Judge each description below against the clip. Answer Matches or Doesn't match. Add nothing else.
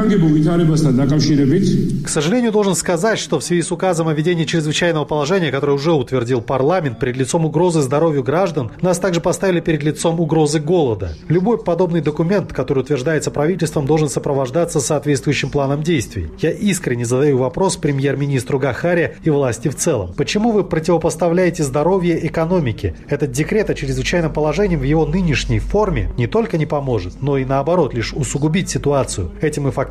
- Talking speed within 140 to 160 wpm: Matches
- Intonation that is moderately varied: Matches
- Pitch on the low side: Doesn't match